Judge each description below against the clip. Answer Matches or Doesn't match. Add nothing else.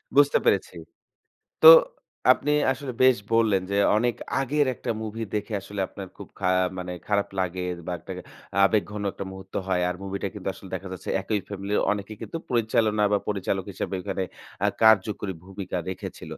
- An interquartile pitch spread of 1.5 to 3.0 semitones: Matches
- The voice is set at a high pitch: Doesn't match